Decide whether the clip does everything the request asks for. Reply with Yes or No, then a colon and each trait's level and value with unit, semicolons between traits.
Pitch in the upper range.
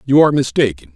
No: low, 130 Hz